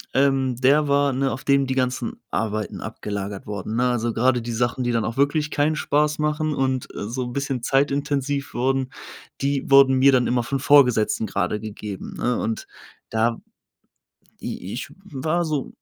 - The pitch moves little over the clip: No, average, 3.1 semitones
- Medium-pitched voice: No, low, 130 Hz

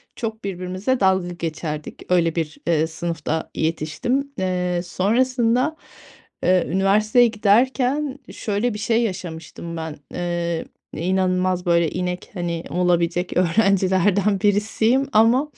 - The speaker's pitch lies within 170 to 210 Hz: Yes, medium, 185 Hz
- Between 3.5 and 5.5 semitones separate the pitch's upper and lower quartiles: Yes, average, 4.3 semitones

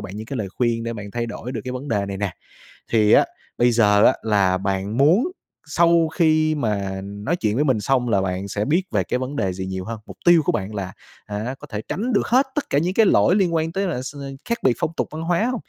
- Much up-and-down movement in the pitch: Yes, wide, 7.9 semitones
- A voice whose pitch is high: No, low, 120 Hz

